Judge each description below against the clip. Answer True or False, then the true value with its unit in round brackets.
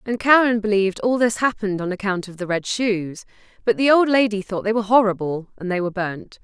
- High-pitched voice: True (210 Hz)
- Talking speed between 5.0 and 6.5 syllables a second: True (6.0 syllables/s)